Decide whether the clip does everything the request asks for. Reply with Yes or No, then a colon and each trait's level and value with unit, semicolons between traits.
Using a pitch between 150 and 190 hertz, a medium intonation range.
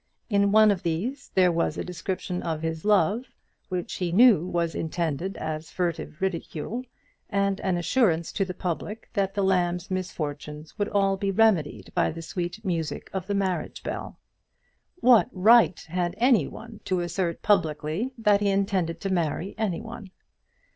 Yes: medium, 185 Hz; average, 3.3 semitones